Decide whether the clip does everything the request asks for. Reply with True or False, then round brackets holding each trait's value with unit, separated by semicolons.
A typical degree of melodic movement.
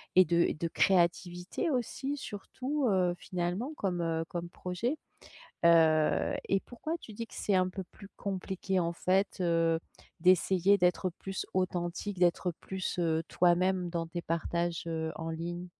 False (2.2 semitones)